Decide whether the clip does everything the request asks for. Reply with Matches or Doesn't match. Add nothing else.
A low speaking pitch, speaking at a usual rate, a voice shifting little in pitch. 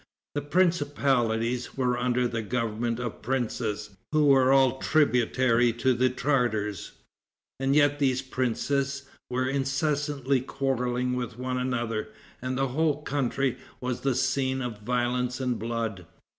Doesn't match